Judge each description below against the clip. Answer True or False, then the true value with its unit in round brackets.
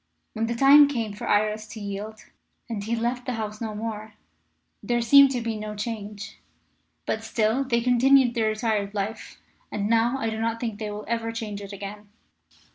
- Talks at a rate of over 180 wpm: True (190 wpm)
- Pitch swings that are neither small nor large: False (1.9 semitones)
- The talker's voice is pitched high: True (220 Hz)